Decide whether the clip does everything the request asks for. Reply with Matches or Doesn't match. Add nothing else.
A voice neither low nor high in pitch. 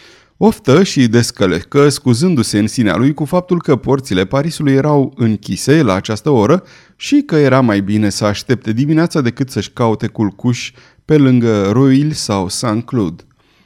Doesn't match